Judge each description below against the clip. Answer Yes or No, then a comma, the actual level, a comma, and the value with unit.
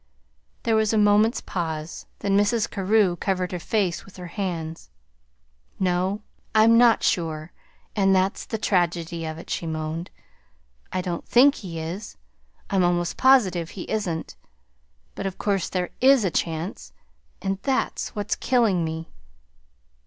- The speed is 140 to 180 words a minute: Yes, average, 145 wpm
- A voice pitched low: No, medium, 185 Hz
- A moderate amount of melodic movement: Yes, average, 3.7 semitones